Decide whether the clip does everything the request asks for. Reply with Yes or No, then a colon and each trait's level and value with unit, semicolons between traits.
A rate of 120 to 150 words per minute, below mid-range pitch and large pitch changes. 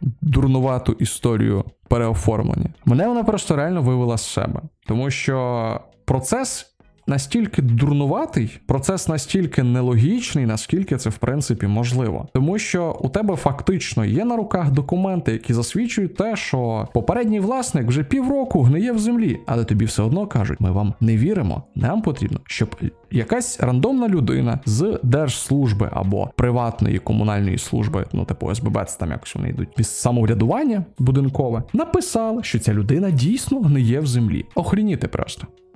Yes: average, 145 wpm; low, 130 Hz; wide, 7.5 semitones